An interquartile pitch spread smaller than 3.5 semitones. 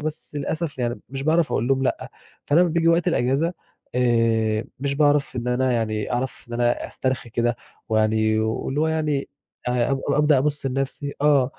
No: average, 3.8 semitones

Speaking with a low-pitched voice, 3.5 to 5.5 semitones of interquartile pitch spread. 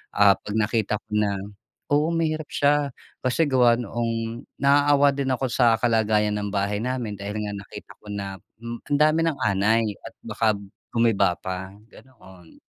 Yes: low, 115 Hz; average, 4.4 semitones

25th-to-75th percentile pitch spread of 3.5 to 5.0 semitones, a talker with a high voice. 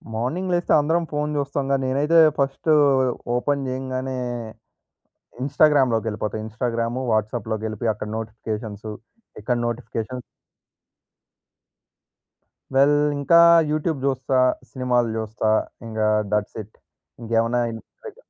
No: average, 4.0 semitones; low, 125 Hz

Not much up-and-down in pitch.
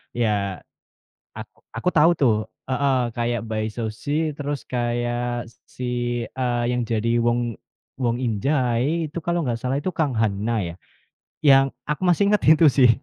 No: average, 3.7 semitones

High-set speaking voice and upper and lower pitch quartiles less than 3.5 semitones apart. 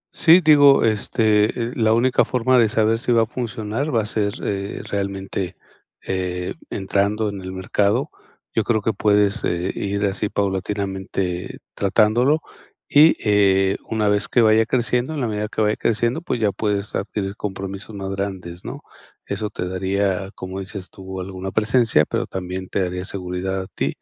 No: low, 100 Hz; average, 2.8 semitones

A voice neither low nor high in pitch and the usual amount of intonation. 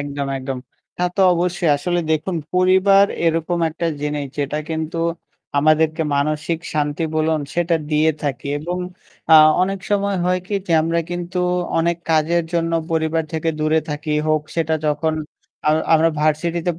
No: medium, 160 Hz; narrow, 2.1 semitones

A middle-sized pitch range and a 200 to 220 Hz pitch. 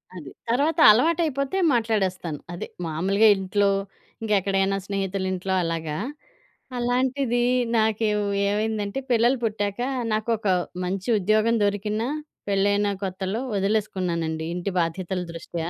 Yes: average, 3.0 semitones; high, 205 Hz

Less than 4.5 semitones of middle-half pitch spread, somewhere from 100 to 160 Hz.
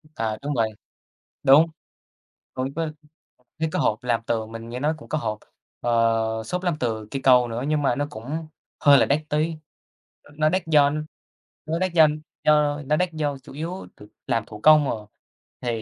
No: average, 5.1 semitones; medium, 140 Hz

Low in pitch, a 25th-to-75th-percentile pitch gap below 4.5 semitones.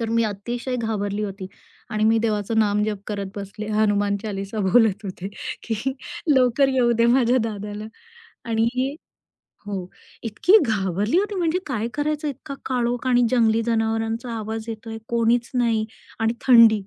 No: high, 225 Hz; narrow, 2.5 semitones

